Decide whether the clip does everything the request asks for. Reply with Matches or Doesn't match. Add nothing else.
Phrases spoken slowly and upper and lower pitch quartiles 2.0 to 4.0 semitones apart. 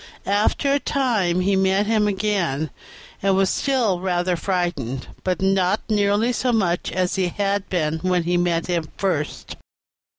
Doesn't match